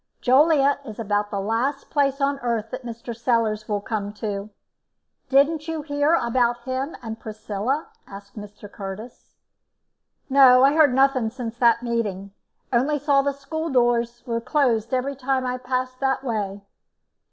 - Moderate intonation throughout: Yes, average, 3.9 semitones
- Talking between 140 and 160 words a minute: Yes, average, 155 wpm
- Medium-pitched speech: No, high, 245 Hz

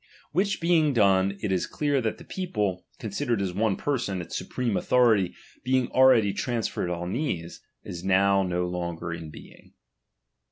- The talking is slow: No, average, 160 wpm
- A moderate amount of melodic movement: No, wide, 5.9 semitones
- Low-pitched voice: Yes, low, 105 Hz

